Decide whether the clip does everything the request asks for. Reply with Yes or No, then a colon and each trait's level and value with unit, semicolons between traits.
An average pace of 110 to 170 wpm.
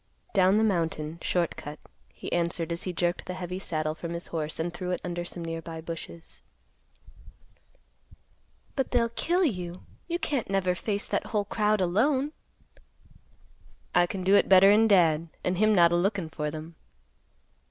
Yes: average, 165 wpm